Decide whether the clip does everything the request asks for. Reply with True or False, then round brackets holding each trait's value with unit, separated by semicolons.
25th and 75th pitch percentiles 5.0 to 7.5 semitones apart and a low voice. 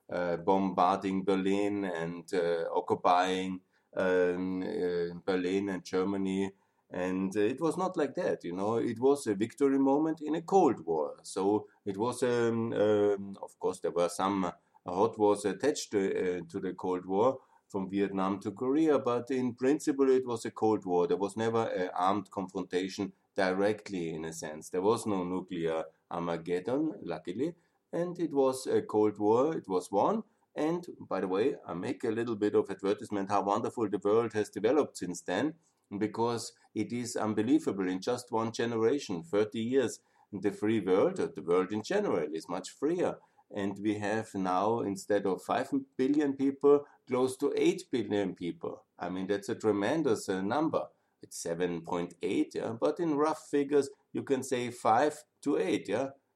True (5.5 semitones; 105 Hz)